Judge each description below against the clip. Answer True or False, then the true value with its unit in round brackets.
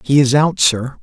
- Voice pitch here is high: False (135 Hz)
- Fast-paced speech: True (235 wpm)